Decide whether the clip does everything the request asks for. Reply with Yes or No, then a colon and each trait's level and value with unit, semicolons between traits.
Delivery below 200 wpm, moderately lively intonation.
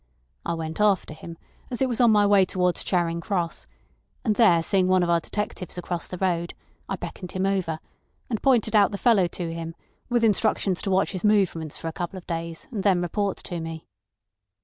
No: fast, 205 wpm; average, 3.4 semitones